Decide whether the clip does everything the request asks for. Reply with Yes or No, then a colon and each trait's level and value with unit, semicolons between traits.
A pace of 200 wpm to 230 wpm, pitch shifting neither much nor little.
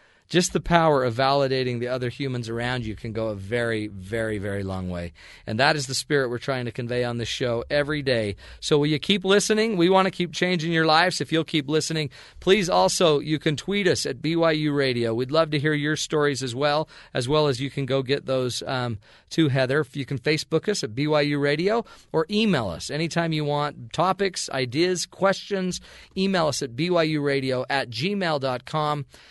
Yes: fast, 205 wpm; average, 4.3 semitones